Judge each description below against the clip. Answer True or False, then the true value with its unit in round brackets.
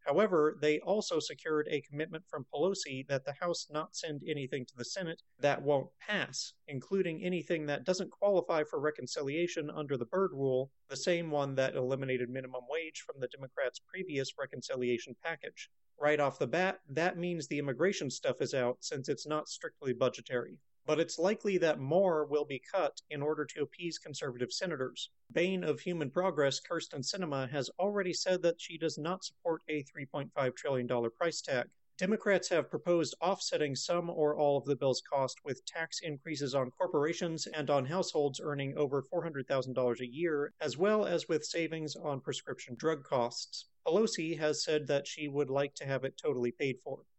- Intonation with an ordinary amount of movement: True (3.8 semitones)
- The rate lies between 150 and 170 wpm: False (185 wpm)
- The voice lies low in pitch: False (150 Hz)